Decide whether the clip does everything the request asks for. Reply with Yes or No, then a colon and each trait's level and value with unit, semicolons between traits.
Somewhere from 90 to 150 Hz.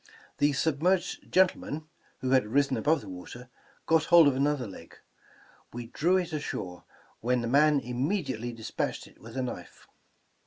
Yes: low, 135 Hz